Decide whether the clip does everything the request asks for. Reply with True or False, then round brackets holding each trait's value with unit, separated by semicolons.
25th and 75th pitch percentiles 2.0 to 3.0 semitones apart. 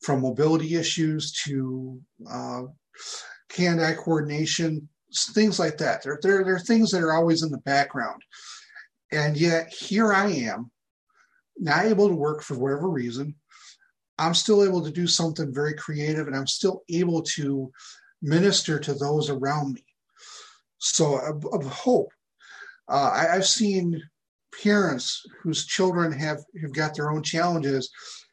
False (4.1 semitones)